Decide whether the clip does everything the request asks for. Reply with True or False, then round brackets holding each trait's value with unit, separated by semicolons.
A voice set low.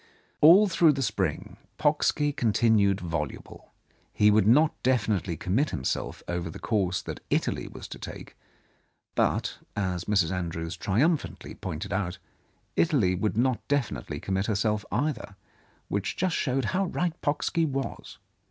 True (105 Hz)